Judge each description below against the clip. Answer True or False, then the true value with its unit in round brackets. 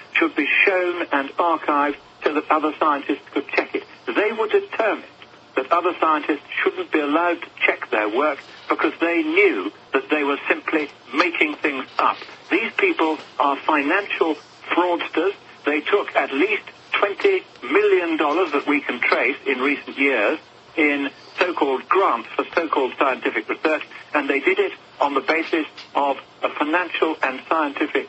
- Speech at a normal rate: True (155 wpm)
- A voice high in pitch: True (320 Hz)